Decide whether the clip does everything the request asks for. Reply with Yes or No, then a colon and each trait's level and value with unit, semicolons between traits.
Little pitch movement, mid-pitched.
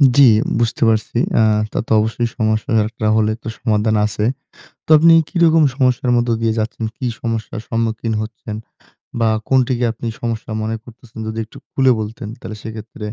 No: narrow, 1.8 semitones; low, 115 Hz